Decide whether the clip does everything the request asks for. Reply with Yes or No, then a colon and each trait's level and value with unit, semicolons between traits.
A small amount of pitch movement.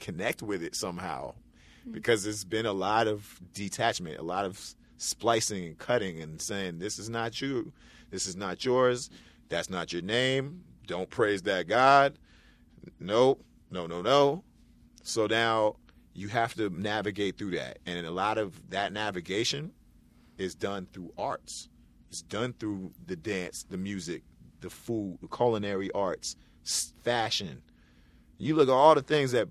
No: average, 4.5 semitones